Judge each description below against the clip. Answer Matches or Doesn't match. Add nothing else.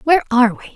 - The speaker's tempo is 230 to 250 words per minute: Matches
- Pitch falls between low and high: Doesn't match